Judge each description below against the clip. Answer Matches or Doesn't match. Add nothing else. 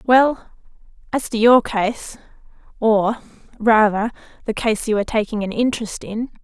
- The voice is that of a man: Doesn't match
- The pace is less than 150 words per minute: Matches